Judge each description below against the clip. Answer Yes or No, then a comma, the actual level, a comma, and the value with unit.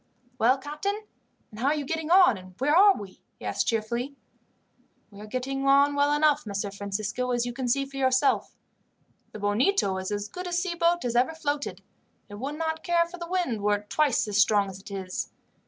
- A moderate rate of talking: No, fast, 210 wpm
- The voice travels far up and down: Yes, wide, 6.8 semitones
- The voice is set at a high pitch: Yes, very high, 260 Hz